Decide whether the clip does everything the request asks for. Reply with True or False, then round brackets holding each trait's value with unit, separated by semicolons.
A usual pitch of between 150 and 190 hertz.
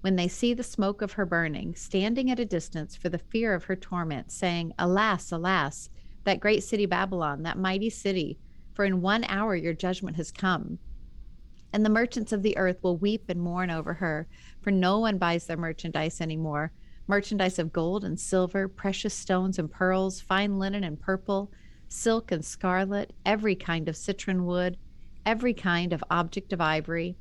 True (185 Hz)